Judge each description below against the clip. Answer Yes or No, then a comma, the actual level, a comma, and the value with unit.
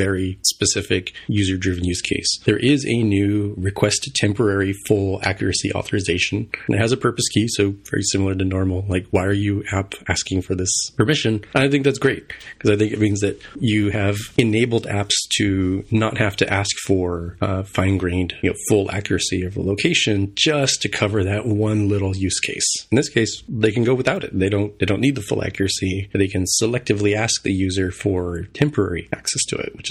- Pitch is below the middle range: Yes, low, 100 Hz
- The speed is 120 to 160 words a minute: No, average, 200 wpm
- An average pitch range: No, narrow, 2.3 semitones